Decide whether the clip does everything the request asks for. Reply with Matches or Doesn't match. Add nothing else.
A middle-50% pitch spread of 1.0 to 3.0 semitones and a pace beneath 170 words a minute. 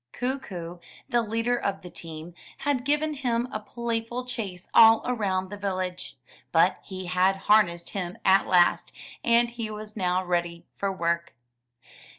Doesn't match